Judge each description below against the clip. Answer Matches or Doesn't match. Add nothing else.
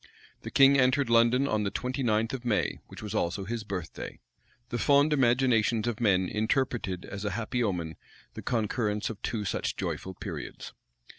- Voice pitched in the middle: Doesn't match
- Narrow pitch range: Doesn't match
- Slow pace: Doesn't match